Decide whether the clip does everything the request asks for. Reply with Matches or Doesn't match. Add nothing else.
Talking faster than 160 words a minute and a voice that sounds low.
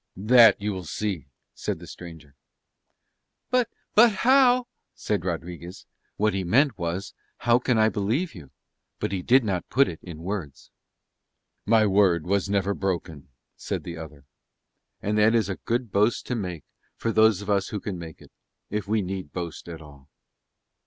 Matches